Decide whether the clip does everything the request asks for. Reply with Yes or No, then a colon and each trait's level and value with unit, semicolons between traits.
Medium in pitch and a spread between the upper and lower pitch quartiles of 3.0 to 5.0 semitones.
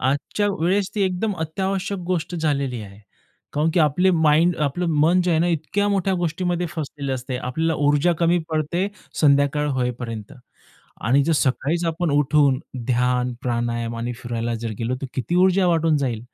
No: medium, 150 Hz; wide, 5.5 semitones